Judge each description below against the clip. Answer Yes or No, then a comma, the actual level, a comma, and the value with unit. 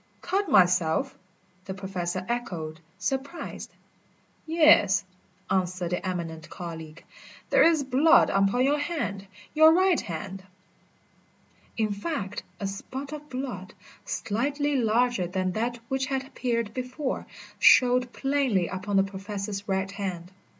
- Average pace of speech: No, slow, 120 wpm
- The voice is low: No, high, 210 Hz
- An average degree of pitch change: No, wide, 6.3 semitones